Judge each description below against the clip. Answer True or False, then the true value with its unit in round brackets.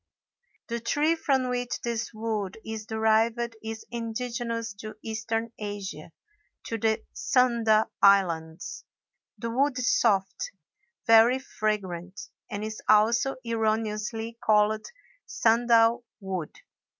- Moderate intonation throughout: False (1.7 semitones)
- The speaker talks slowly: True (105 wpm)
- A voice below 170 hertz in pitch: False (225 Hz)